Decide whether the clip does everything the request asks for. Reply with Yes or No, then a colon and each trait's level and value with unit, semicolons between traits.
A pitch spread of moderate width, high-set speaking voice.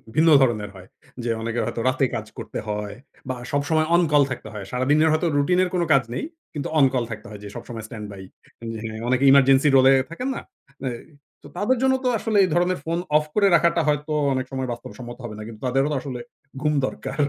No: average, 5.0 semitones; low, 135 Hz